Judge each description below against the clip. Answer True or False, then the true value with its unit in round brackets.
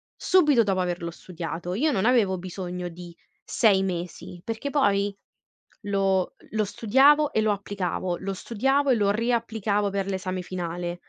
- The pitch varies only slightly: False (3.9 semitones)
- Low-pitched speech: False (200 Hz)